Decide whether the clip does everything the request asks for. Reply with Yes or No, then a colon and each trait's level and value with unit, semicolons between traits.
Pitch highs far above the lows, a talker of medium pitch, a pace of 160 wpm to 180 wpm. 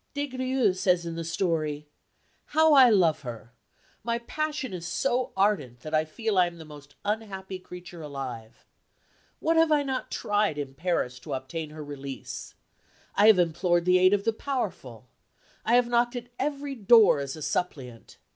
Yes: wide, 7.9 semitones; medium, 180 Hz; average, 175 wpm